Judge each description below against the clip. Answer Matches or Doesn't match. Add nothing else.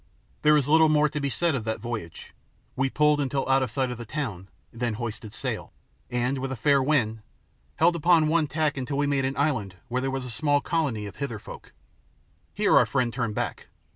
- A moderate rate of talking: Doesn't match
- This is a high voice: Doesn't match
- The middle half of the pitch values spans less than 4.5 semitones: Matches